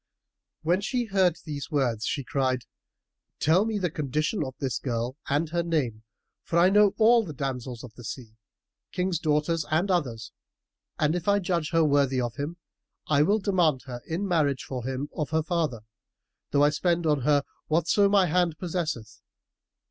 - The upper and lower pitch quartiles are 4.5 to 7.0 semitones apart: Yes, average, 4.9 semitones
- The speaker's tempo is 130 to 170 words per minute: No, average, 180 wpm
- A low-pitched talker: No, medium, 155 Hz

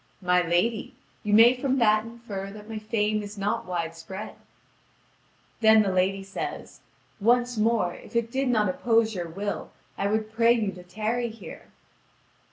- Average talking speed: Yes, average, 160 wpm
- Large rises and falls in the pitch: No, average, 2.9 semitones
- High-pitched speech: Yes, high, 215 Hz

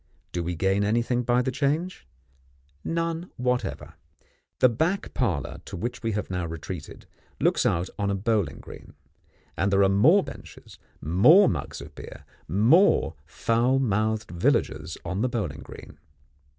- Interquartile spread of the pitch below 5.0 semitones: No, wide, 5.6 semitones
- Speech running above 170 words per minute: No, average, 150 wpm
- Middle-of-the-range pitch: No, low, 110 Hz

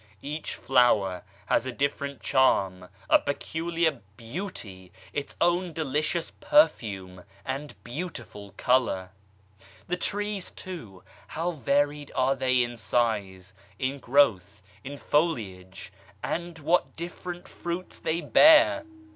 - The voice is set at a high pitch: No, medium, 140 Hz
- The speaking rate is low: Yes, slow, 110 wpm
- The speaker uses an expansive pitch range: Yes, wide, 7.6 semitones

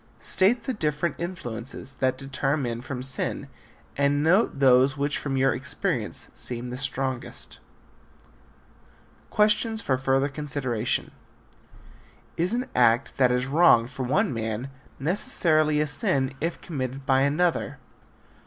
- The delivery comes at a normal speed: No, slow, 125 wpm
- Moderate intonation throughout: Yes, average, 3.4 semitones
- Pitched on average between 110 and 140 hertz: Yes, low, 135 Hz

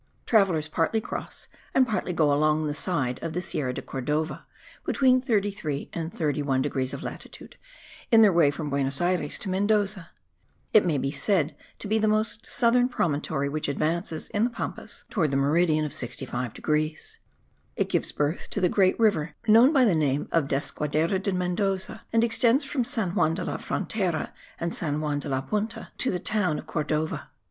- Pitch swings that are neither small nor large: No, wide, 5.9 semitones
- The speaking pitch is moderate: Yes, medium, 170 Hz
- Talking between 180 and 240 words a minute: Yes, average, 185 wpm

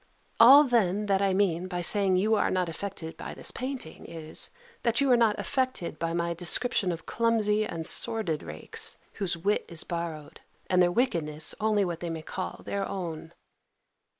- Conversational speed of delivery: Yes, average, 175 wpm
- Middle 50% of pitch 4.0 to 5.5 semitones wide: Yes, average, 4.3 semitones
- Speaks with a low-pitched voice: No, medium, 185 Hz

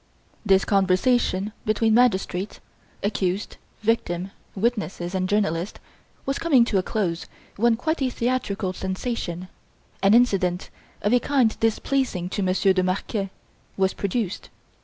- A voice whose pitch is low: No, high, 200 Hz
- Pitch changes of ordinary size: Yes, average, 4.0 semitones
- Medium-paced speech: No, slow, 125 wpm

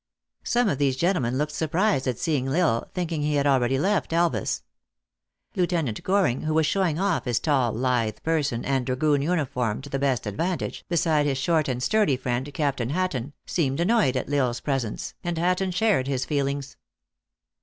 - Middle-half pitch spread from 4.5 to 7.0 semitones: Yes, average, 4.8 semitones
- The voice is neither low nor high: Yes, medium, 145 Hz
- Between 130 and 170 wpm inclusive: No, average, 180 wpm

